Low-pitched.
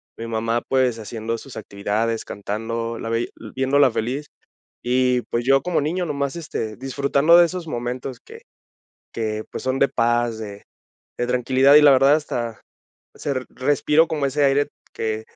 Yes: low, 125 Hz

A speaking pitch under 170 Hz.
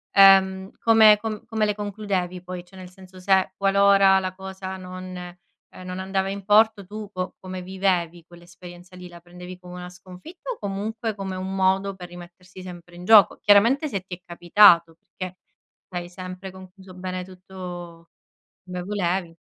No: medium, 185 Hz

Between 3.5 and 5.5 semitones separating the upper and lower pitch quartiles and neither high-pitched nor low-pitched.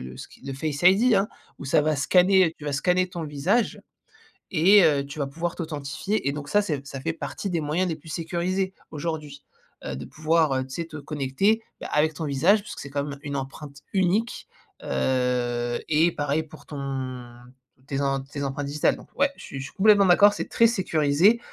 Yes: average, 4.5 semitones; medium, 155 Hz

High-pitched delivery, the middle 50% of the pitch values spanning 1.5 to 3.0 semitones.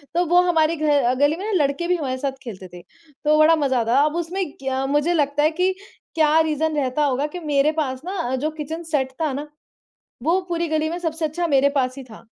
No: very high, 300 Hz; average, 3.4 semitones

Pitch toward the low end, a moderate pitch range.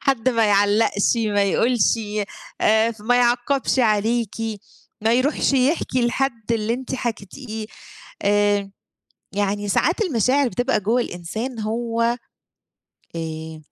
No: high, 230 Hz; average, 3.3 semitones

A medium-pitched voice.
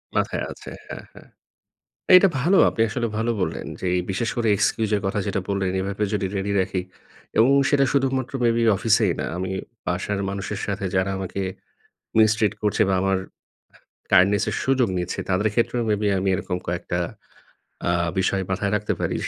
No: low, 100 Hz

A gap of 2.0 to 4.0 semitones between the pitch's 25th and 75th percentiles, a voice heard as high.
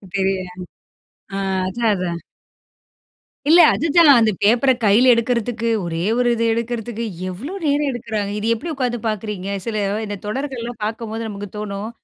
Yes: average, 3.0 semitones; high, 225 Hz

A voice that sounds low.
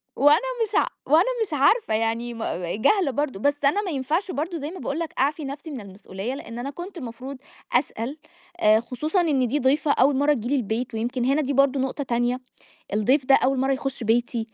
No: very high, 270 Hz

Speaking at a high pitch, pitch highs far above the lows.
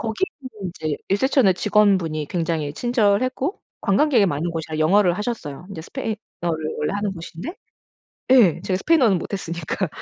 Yes: high, 195 Hz; wide, 6.0 semitones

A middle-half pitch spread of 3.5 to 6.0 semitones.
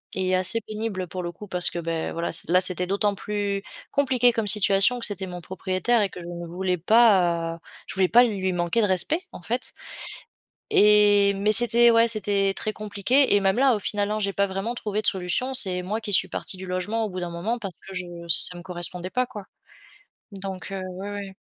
No: average, 2.8 semitones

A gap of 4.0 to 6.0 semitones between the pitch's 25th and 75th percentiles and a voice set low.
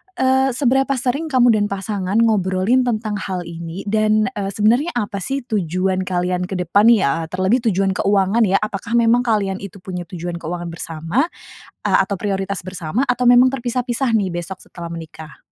No: average, 4.6 semitones; high, 200 Hz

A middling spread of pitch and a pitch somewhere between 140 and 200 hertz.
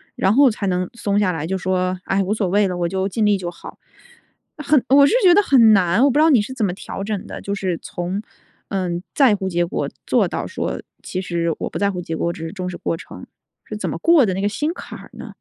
Yes: average, 3.7 semitones; high, 195 Hz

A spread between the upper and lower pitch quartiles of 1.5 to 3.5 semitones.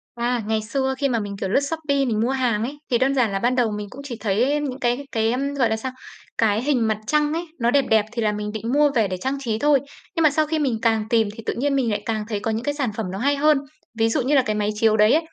No: average, 4.2 semitones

